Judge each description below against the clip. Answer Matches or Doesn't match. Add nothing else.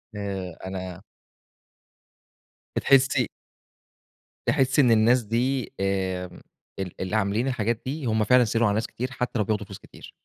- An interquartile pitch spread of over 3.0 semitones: Matches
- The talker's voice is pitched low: Matches